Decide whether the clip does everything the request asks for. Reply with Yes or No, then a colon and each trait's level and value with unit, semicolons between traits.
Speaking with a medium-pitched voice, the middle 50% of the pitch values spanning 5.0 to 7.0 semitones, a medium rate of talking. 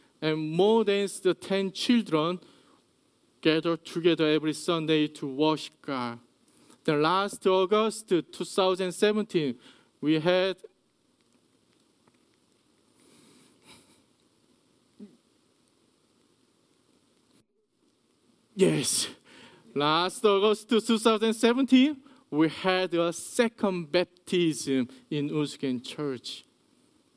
No: medium, 180 Hz; wide, 5.4 semitones; slow, 70 wpm